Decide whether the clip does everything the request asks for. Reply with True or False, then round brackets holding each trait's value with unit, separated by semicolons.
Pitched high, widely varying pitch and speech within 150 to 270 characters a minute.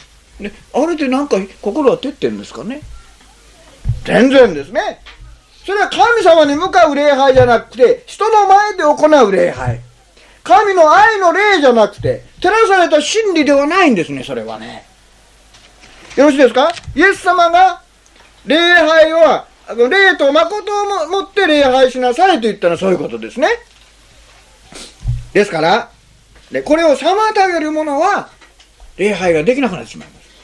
False (310 Hz; 7.4 semitones; 280 characters per minute)